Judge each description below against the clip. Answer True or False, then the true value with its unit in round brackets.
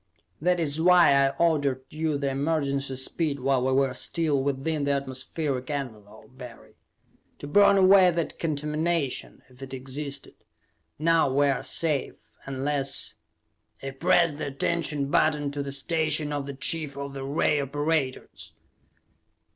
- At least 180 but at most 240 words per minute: False (140 wpm)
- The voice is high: False (140 Hz)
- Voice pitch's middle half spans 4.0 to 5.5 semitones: False (2.7 semitones)